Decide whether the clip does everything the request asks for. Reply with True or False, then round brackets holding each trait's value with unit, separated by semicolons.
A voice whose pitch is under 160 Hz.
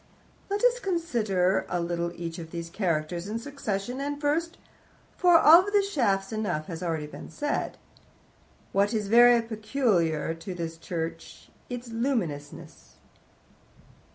False (205 Hz)